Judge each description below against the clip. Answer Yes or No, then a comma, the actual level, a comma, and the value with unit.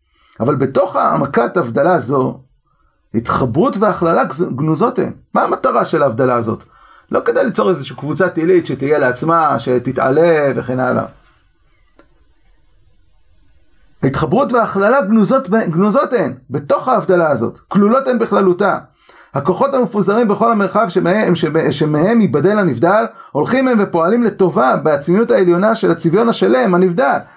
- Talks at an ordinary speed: Yes, average, 125 wpm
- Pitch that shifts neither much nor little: No, wide, 6.6 semitones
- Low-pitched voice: No, medium, 185 Hz